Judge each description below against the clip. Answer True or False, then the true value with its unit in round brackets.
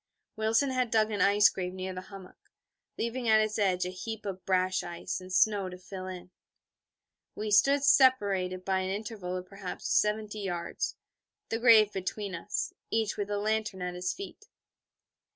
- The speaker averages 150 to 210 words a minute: True (170 wpm)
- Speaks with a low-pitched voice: False (200 Hz)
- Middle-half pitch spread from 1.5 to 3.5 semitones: True (2.8 semitones)